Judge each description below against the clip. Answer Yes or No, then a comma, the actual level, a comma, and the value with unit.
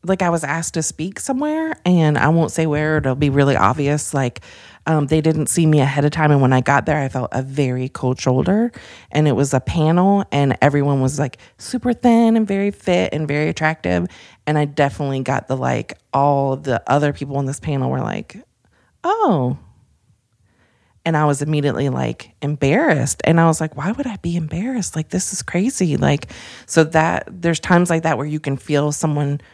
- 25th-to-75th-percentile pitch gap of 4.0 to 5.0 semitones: No, average, 3.4 semitones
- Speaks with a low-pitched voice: No, medium, 150 Hz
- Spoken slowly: No, fast, 205 wpm